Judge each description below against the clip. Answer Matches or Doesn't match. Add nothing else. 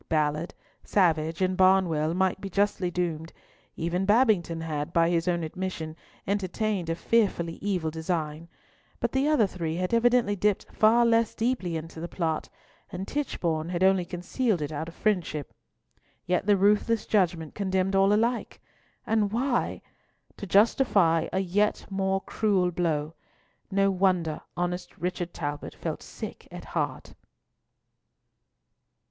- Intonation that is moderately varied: Matches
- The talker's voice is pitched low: Doesn't match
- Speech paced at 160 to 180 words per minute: Doesn't match